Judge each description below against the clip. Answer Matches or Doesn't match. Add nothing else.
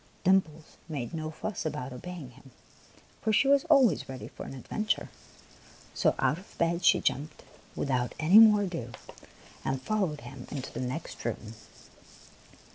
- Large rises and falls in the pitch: Matches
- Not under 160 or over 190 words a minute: Doesn't match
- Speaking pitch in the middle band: Matches